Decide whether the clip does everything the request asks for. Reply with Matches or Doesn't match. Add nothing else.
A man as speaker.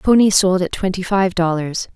Doesn't match